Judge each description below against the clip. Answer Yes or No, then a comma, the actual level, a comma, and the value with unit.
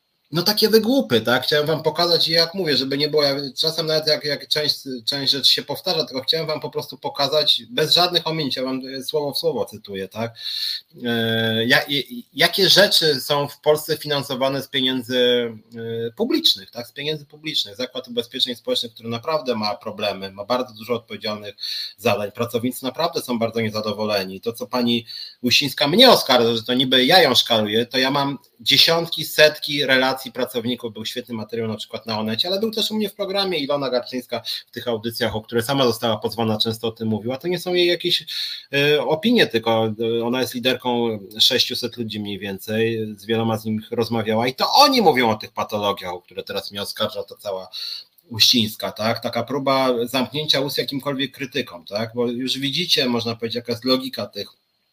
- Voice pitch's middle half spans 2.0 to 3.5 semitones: No, average, 4.8 semitones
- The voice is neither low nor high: No, low, 130 Hz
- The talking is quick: Yes, fast, 185 wpm